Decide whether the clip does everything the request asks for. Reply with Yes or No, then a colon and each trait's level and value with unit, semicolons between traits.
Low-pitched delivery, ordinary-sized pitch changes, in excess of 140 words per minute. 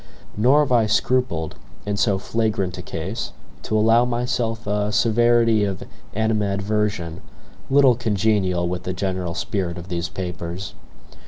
No: low, 105 Hz; average, 3.8 semitones; slow, 135 wpm